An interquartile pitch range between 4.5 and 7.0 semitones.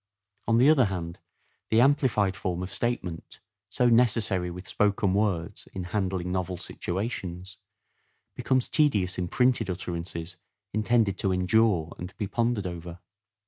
No: average, 4.1 semitones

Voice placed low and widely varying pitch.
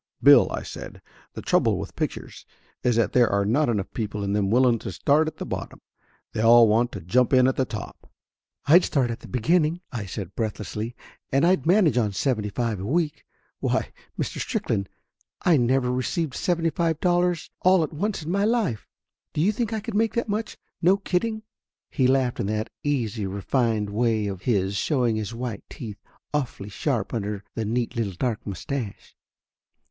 Yes: low, 125 Hz; wide, 6.9 semitones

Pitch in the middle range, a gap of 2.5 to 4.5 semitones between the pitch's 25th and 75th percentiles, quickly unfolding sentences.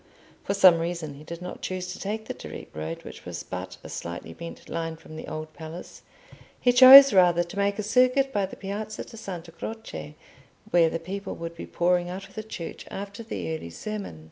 Yes: medium, 180 Hz; average, 3.9 semitones; fast, 210 wpm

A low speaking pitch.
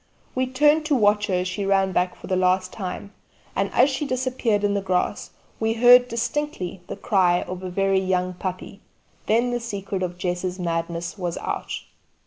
No: high, 195 Hz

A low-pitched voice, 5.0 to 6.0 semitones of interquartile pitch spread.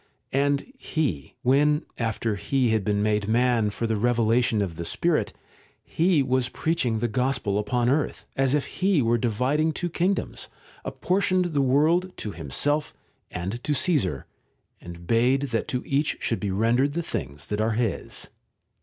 Yes: low, 125 Hz; wide, 5.4 semitones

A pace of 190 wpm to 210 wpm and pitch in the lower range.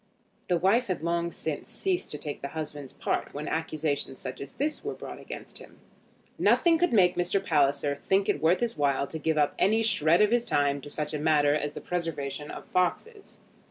No: fast, 205 wpm; medium, 160 Hz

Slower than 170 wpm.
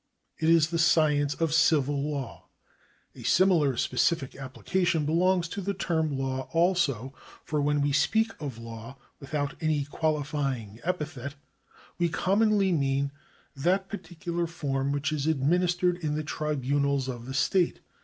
Yes: average, 145 wpm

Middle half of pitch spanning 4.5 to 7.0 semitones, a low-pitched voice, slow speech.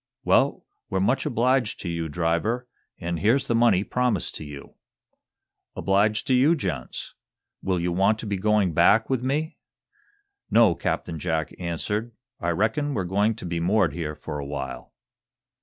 No: wide, 5.6 semitones; low, 100 Hz; average, 160 wpm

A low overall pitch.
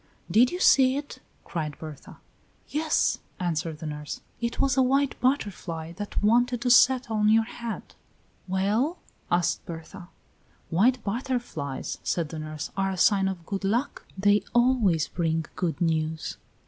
No: high, 200 Hz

